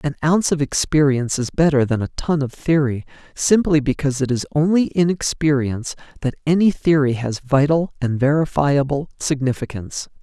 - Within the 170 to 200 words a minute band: No, average, 155 wpm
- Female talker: No, male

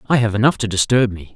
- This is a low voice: Yes, low, 110 Hz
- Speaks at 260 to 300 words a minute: Yes, fast, 265 wpm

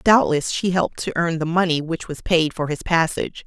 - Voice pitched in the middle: Yes, medium, 165 Hz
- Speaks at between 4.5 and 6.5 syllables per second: Yes, 5.4 syllables/s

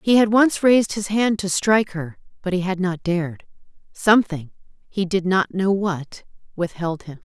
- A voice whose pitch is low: No, high, 190 Hz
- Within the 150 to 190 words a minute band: Yes, average, 165 wpm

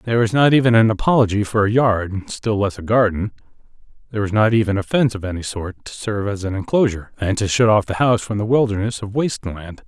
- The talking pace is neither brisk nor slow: No, fast, 230 wpm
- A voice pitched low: Yes, low, 105 Hz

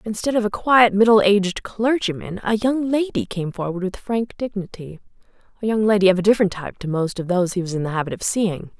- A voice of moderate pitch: No, high, 200 Hz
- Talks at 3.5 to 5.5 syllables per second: No, 6.0 syllables/s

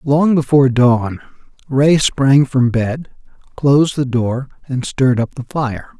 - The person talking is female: No, male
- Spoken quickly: No, average, 150 wpm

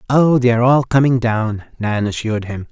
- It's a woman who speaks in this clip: No, male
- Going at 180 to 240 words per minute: Yes, average, 200 wpm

